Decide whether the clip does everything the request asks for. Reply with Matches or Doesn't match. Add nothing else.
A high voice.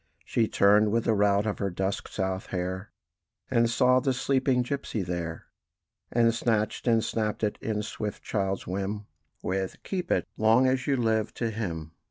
Doesn't match